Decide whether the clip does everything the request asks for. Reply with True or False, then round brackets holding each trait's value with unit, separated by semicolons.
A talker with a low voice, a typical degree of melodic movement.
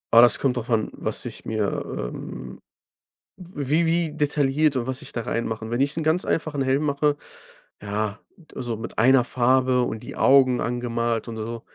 True (125 Hz; 3.8 semitones)